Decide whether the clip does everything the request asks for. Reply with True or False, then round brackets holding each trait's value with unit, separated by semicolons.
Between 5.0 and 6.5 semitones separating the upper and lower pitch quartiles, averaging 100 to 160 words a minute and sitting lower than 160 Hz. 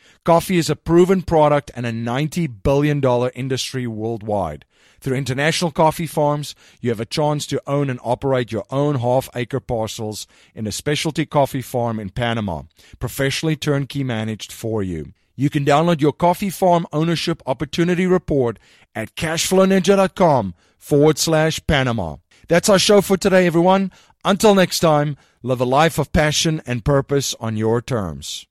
True (5.5 semitones; 155 wpm; 140 Hz)